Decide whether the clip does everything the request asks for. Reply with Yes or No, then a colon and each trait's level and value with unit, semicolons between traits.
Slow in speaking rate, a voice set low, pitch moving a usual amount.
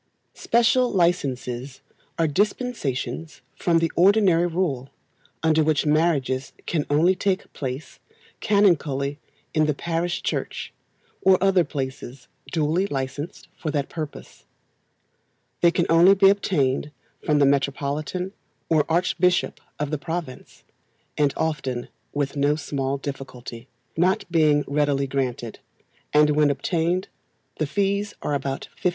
No: slow, 120 wpm; medium, 155 Hz; average, 4.1 semitones